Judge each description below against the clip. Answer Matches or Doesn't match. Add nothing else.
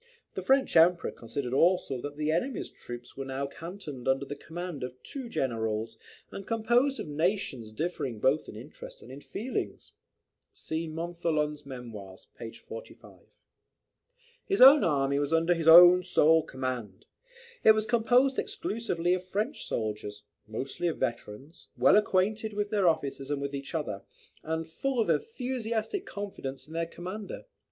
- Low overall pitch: Doesn't match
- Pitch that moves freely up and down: Matches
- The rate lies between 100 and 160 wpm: Matches